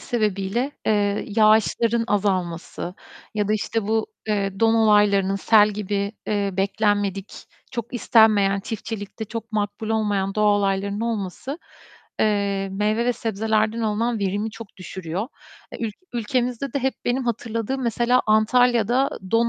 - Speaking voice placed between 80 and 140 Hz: No, high, 215 Hz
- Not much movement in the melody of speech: Yes, narrow, 2.3 semitones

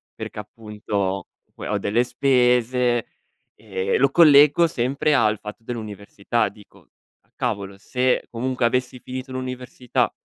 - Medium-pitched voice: No, low, 120 Hz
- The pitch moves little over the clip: No, average, 3.4 semitones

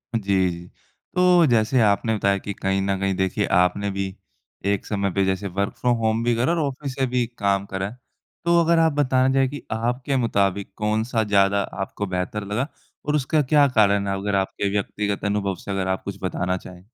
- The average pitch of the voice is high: No, low, 100 Hz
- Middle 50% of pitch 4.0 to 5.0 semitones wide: Yes, average, 4.4 semitones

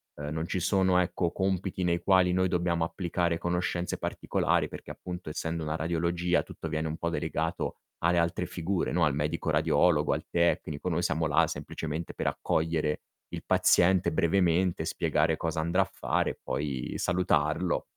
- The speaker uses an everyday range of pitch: No, narrow, 1.9 semitones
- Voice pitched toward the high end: No, very low, 85 Hz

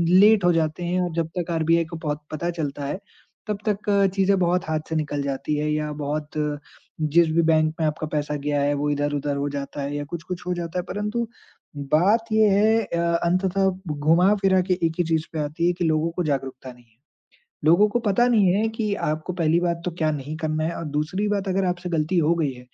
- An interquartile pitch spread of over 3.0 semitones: Yes, average, 3.6 semitones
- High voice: No, medium, 165 Hz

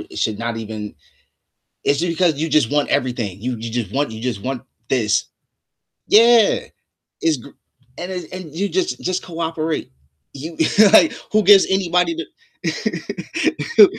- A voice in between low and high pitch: Yes, medium, 160 Hz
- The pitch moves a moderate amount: No, wide, 7.6 semitones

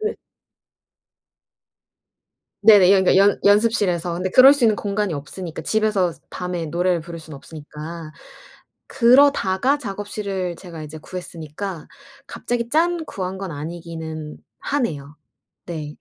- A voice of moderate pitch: Yes, medium, 180 Hz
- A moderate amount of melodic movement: Yes, average, 4.6 semitones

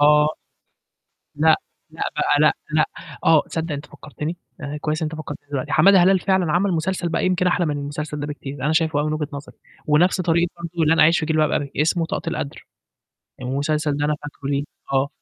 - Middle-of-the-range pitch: Yes, medium, 155 Hz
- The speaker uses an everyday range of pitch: No, narrow, 2.2 semitones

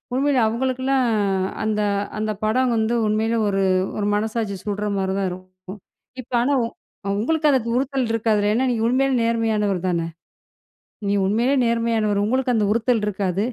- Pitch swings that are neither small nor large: Yes, average, 3.4 semitones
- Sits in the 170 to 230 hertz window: Yes, high, 225 Hz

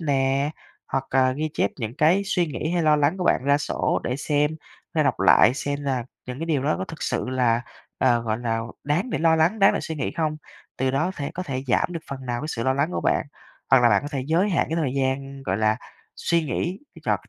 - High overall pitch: No, medium, 140 Hz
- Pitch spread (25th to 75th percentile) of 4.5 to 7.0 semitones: No, average, 3.7 semitones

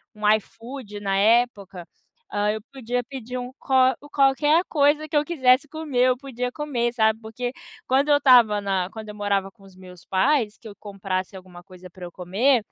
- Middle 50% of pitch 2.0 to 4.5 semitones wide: No, average, 4.9 semitones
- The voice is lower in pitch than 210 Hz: No, high, 230 Hz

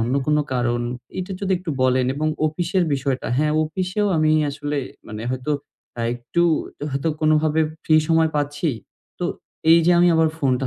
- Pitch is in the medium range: Yes, medium, 150 Hz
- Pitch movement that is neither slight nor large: Yes, average, 3.9 semitones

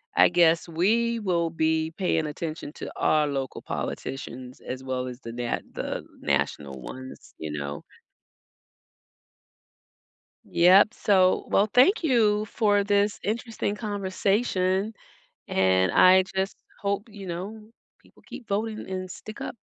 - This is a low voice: No, medium, 185 Hz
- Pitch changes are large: Yes, wide, 6.2 semitones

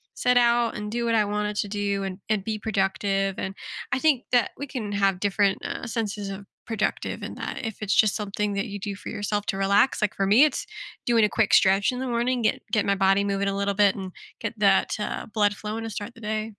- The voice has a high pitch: Yes, high, 210 Hz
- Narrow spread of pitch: Yes, narrow, 2.2 semitones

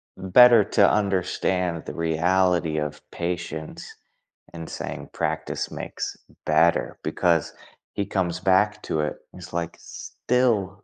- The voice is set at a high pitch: No, very low, 90 Hz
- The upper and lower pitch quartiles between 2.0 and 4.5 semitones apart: Yes, average, 2.7 semitones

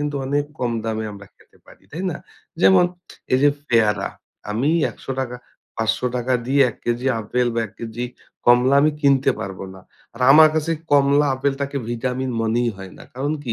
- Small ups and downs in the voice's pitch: No, average, 3.6 semitones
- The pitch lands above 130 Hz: No, low, 125 Hz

